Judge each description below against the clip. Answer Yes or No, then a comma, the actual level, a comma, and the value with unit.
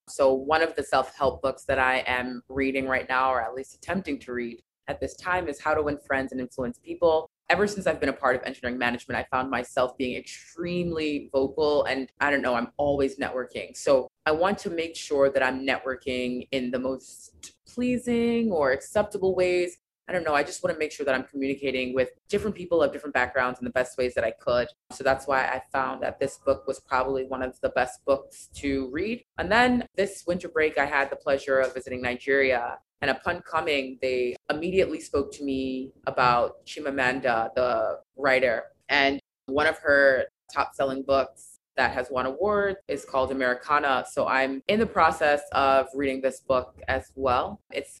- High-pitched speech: No, low, 135 Hz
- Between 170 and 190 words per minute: No, average, 200 wpm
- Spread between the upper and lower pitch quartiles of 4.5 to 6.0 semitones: No, average, 3.4 semitones